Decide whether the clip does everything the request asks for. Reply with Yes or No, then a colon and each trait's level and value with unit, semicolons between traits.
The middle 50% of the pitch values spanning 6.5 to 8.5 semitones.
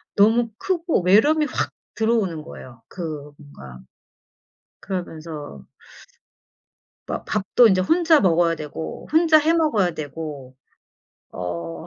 Yes: wide, 8.1 semitones